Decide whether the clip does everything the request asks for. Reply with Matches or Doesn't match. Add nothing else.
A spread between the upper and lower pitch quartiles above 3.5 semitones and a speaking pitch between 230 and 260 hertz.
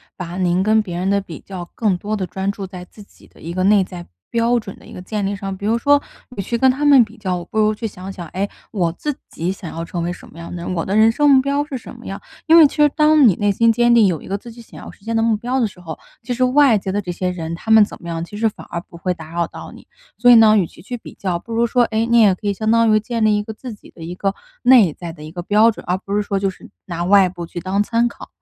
Doesn't match